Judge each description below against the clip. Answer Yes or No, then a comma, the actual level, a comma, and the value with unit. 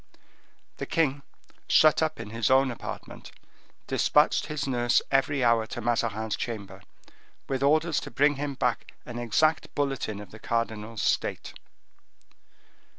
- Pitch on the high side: No, low, 120 Hz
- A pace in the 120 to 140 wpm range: Yes, slow, 135 wpm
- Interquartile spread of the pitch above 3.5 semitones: Yes, average, 4.0 semitones